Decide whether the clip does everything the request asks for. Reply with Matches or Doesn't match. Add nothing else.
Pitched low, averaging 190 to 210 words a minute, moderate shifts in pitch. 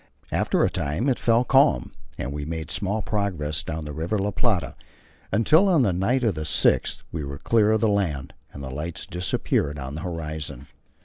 Doesn't match